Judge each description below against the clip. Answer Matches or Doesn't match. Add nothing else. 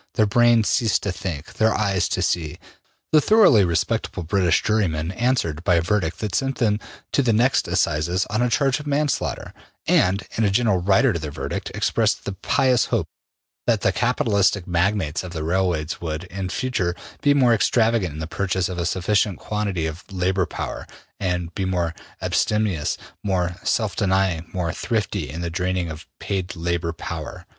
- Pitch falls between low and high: Doesn't match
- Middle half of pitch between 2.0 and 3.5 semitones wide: Doesn't match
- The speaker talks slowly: Doesn't match